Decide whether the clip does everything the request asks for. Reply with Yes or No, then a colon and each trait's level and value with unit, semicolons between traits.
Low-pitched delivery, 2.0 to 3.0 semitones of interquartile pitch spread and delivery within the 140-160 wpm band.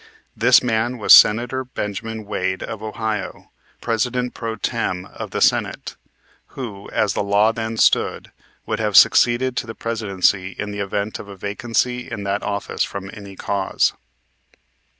Yes: low, 110 Hz; narrow, 2.6 semitones; average, 150 wpm